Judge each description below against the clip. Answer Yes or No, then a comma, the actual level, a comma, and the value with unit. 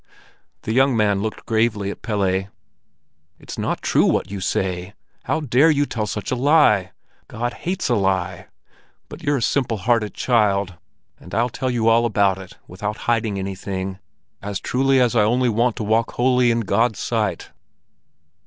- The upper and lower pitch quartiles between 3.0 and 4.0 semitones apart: Yes, average, 3.6 semitones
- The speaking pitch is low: Yes, low, 110 Hz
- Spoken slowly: No, average, 170 wpm